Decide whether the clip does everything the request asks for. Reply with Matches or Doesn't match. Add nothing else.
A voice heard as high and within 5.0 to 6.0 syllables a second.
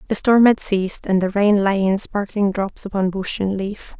Doesn't match